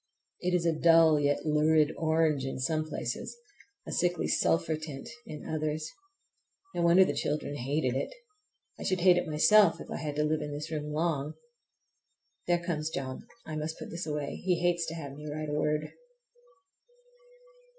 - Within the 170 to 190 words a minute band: Yes, average, 175 wpm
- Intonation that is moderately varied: No, narrow, 1.8 semitones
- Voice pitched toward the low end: No, medium, 155 Hz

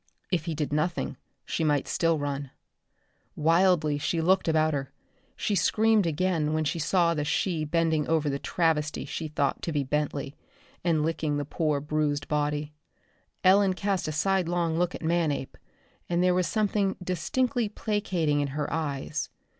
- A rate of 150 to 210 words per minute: Yes, average, 160 wpm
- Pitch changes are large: No, average, 3.2 semitones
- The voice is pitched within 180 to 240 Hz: No, medium, 160 Hz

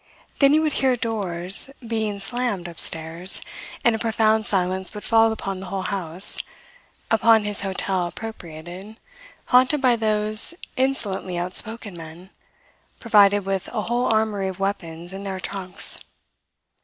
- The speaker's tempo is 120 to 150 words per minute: Yes, slow, 135 wpm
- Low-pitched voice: No, high, 200 Hz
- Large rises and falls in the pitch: No, average, 3.3 semitones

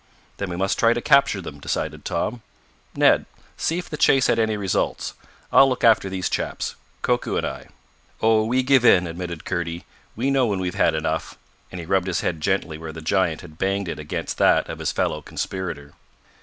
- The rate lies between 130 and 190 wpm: No, average, 200 wpm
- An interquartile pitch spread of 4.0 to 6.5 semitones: Yes, average, 5.2 semitones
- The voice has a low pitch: Yes, very low, 95 Hz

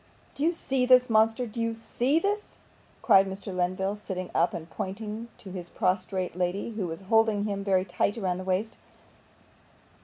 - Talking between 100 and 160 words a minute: No, average, 175 wpm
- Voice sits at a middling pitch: No, high, 200 Hz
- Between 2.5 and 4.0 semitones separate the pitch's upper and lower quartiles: Yes, average, 3.6 semitones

